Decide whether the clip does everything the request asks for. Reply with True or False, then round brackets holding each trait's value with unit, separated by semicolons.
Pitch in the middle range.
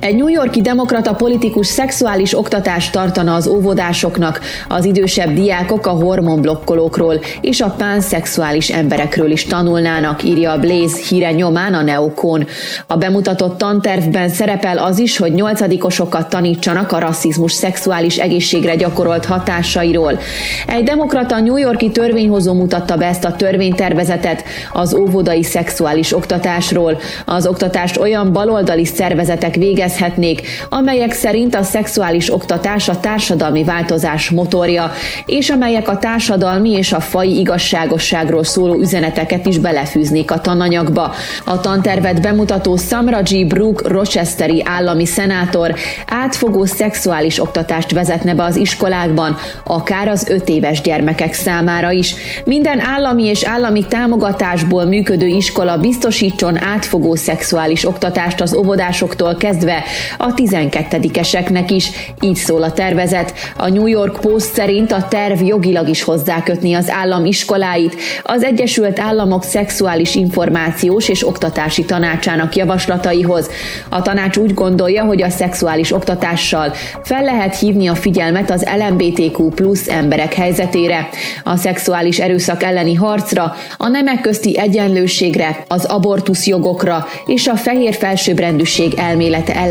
True (180 Hz)